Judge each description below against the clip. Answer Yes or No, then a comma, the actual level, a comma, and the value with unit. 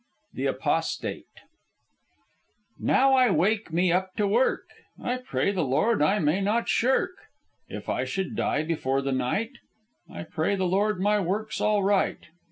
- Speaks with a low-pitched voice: No, high, 195 Hz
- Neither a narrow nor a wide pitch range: Yes, average, 4.7 semitones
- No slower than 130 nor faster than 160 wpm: Yes, average, 155 wpm